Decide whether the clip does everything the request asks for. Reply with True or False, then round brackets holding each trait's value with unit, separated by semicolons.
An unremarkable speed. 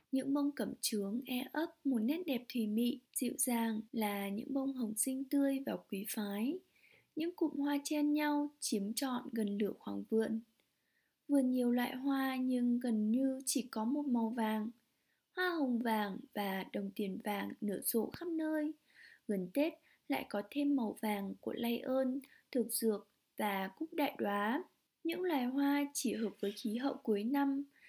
True (175 wpm)